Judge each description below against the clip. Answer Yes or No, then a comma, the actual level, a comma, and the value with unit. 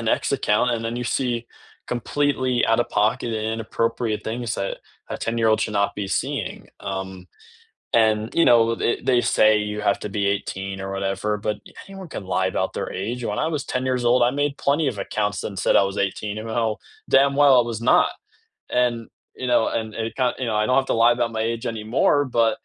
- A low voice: Yes, low, 115 Hz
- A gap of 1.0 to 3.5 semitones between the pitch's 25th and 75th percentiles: Yes, average, 2.9 semitones